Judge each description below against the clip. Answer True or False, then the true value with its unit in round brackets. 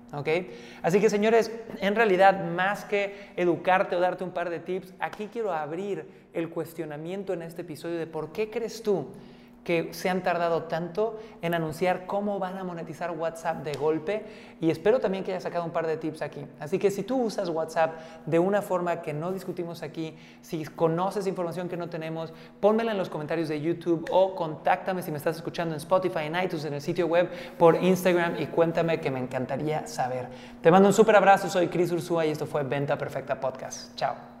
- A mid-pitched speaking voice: True (175 Hz)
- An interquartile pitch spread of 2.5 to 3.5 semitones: True (3.0 semitones)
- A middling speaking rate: False (200 wpm)